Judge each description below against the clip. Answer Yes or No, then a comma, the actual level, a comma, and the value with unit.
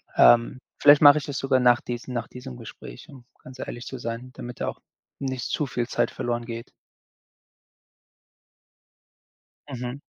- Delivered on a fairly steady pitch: Yes, narrow, 1.9 semitones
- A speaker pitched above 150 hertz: No, low, 125 Hz